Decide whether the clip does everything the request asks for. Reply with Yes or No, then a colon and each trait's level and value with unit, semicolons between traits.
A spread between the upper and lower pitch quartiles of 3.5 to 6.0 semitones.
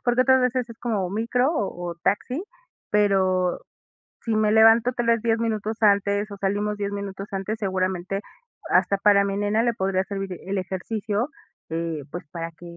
No: average, 2.8 semitones